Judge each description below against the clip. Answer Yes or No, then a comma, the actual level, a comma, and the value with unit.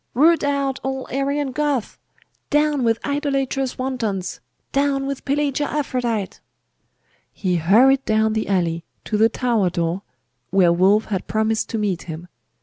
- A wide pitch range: Yes, wide, 5.7 semitones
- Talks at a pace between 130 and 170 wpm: Yes, average, 140 wpm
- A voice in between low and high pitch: No, high, 245 Hz